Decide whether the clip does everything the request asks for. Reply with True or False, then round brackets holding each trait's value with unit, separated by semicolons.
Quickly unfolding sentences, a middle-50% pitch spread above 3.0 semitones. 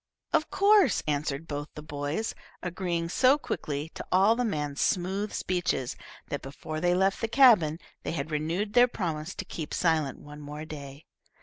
False (170 wpm; 5.2 semitones)